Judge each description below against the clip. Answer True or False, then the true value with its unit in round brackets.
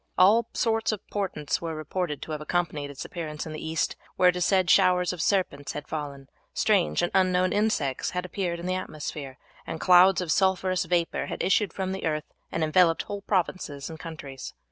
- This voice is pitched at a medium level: True (175 Hz)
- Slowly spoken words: False (195 wpm)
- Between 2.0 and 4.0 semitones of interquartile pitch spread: True (3.4 semitones)